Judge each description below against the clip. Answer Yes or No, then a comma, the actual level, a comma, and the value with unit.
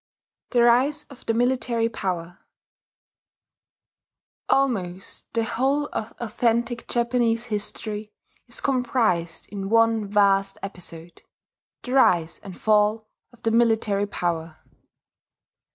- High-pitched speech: Yes, high, 225 Hz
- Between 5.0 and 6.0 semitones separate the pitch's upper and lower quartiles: No, average, 3.4 semitones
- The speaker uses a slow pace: Yes, slow, 105 wpm